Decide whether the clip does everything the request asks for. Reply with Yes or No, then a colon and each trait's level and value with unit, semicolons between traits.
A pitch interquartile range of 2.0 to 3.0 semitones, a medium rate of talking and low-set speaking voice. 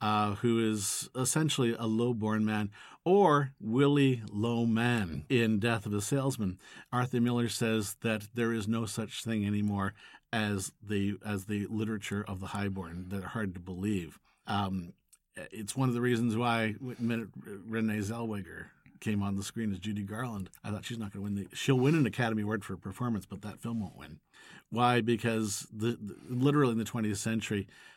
Yes: narrow, 2.6 semitones; average, 180 wpm; low, 110 Hz